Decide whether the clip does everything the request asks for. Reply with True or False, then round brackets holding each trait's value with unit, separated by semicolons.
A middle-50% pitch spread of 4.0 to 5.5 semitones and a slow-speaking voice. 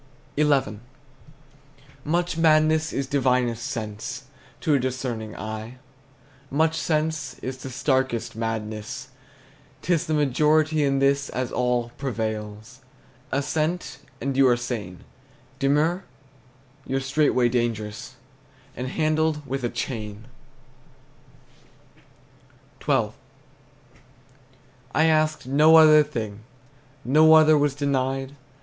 True (4.3 semitones; 100 wpm)